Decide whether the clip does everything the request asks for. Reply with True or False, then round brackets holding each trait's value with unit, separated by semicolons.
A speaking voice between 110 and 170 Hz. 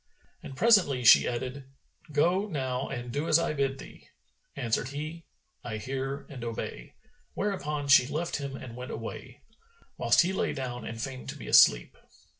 True (135 Hz)